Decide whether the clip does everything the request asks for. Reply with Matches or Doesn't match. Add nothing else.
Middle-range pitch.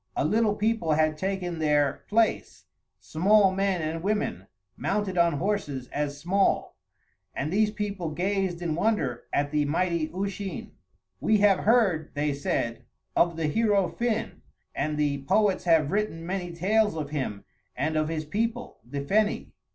Matches